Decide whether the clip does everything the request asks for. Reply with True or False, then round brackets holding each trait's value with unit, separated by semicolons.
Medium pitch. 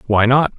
False (120 Hz)